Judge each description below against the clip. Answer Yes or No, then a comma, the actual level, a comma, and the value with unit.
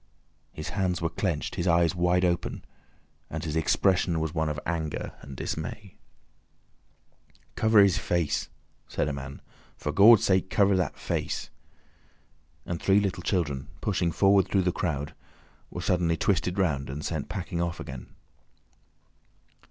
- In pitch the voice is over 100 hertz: No, very low, 85 Hz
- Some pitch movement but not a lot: Yes, average, 3.3 semitones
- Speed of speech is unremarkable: Yes, average, 145 wpm